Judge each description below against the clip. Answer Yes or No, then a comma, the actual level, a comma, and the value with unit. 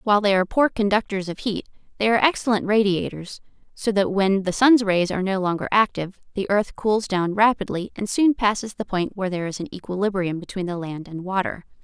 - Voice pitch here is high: Yes, high, 200 Hz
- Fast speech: Yes, fast, 210 wpm